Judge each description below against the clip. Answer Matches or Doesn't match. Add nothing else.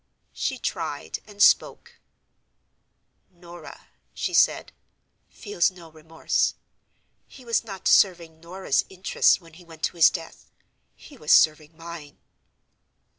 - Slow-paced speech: Matches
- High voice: Doesn't match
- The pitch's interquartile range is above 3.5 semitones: Doesn't match